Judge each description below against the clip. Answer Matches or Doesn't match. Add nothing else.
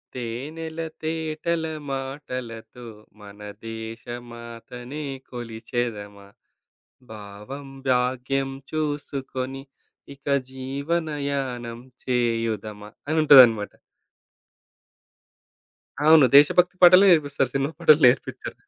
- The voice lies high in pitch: Doesn't match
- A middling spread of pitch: Matches